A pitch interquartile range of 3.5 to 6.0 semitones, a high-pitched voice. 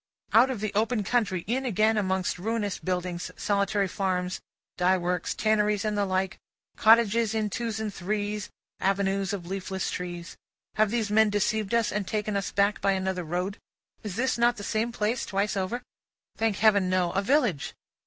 No: narrow, 2.5 semitones; high, 205 Hz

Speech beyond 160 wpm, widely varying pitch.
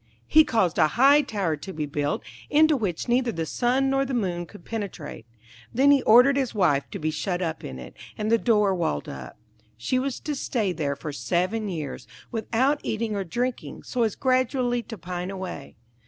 Yes: average, 195 wpm; wide, 6.9 semitones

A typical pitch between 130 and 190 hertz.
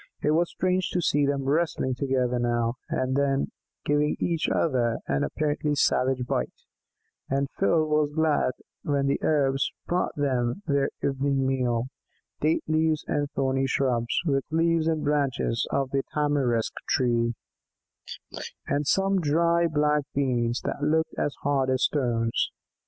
Yes: medium, 140 Hz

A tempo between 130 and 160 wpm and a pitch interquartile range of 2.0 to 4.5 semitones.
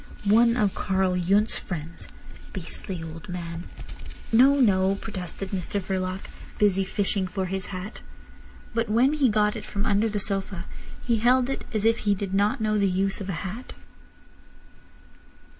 Yes: average, 155 wpm; average, 2.7 semitones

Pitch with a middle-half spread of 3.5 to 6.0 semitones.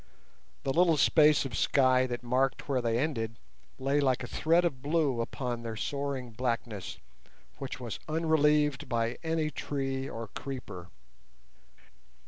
Yes: average, 3.8 semitones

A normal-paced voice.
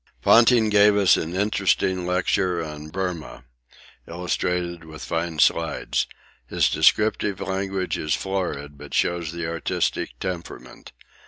No: slow, 115 wpm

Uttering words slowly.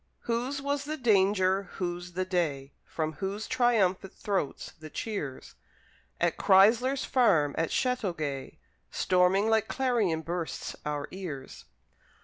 Yes: slow, 120 wpm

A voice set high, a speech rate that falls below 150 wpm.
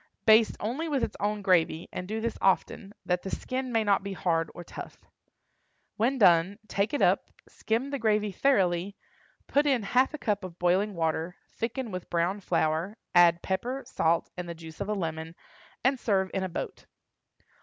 No: high, 195 Hz; average, 185 wpm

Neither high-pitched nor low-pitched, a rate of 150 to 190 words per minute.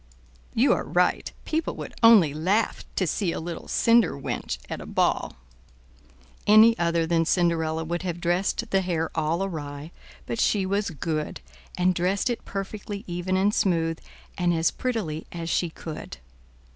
Yes: medium, 175 Hz; average, 160 wpm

